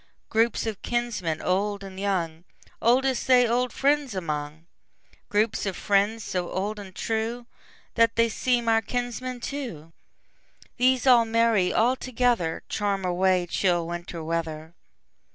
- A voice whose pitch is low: No, high, 210 Hz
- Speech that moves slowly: Yes, slow, 115 wpm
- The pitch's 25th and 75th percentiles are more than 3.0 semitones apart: Yes, average, 5.0 semitones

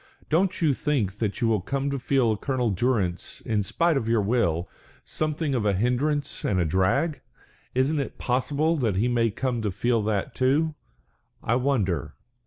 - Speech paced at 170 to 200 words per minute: Yes, average, 175 wpm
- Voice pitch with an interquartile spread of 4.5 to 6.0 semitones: Yes, average, 5.3 semitones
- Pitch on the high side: No, low, 125 Hz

